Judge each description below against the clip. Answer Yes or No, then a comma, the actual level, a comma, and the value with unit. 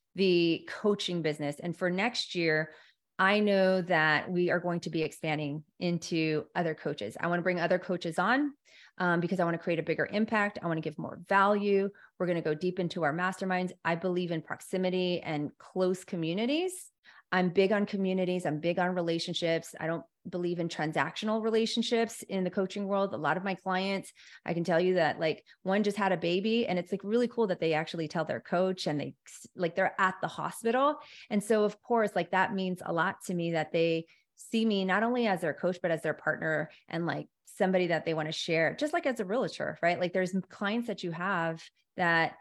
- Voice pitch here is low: No, medium, 180 Hz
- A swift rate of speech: Yes, fast, 215 wpm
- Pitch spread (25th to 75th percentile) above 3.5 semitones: No, average, 3.1 semitones